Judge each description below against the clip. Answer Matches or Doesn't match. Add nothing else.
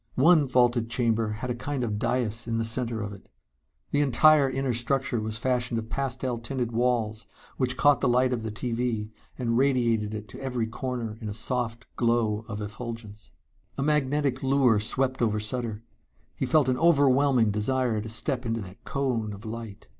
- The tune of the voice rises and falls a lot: Doesn't match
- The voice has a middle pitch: Doesn't match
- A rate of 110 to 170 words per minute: Doesn't match